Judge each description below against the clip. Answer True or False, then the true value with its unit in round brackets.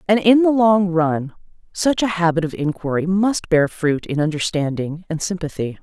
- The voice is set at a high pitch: False (175 Hz)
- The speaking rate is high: False (175 wpm)